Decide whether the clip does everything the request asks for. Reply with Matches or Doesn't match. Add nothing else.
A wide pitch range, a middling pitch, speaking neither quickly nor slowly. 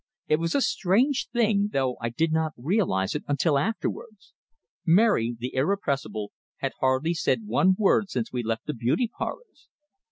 Matches